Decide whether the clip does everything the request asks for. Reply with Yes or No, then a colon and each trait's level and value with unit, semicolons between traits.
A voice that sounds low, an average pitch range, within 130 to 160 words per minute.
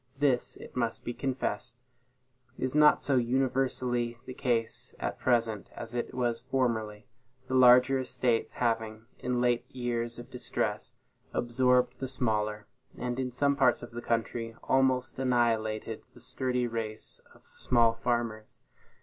No: low, 120 Hz; narrow, 1.9 semitones; average, 140 wpm